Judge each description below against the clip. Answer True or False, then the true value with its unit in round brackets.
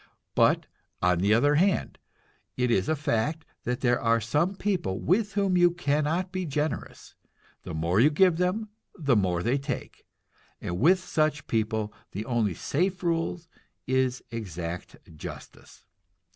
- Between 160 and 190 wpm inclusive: False (145 wpm)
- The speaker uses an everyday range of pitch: False (8.0 semitones)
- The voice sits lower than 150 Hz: True (140 Hz)